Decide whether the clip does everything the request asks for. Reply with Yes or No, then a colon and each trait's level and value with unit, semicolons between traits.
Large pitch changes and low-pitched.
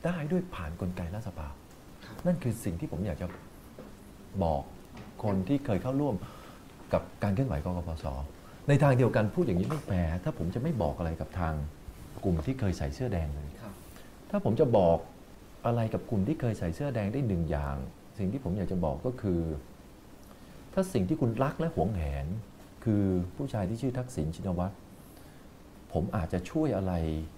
Yes: wide, 6.0 semitones; very low, 95 Hz